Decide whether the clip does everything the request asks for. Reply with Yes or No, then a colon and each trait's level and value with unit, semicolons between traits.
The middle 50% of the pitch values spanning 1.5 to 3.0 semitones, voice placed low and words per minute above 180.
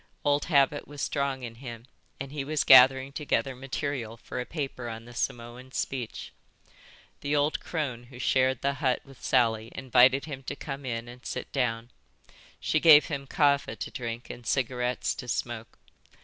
No: narrow, 2.5 semitones; low, 130 Hz; average, 170 wpm